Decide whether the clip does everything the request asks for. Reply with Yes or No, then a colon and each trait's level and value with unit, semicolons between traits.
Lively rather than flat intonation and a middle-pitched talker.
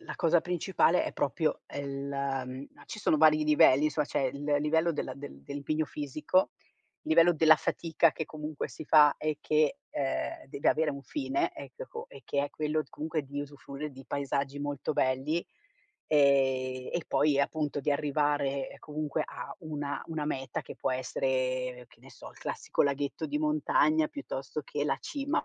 No: narrow, 2.1 semitones; medium, 145 Hz